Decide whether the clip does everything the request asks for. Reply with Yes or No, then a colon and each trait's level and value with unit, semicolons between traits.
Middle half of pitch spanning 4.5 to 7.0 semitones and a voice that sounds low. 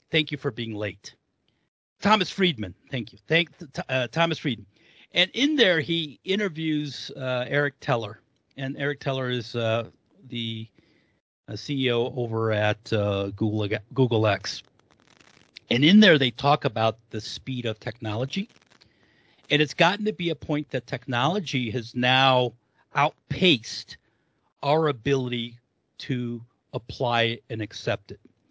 Yes: average, 4.8 semitones; low, 130 Hz